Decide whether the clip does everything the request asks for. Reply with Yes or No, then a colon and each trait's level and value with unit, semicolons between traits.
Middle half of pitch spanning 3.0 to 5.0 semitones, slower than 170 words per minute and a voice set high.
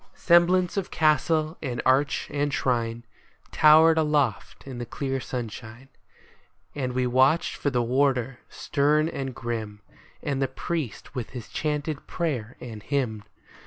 No: average, 4.0 semitones; slow, 135 wpm; low, 135 Hz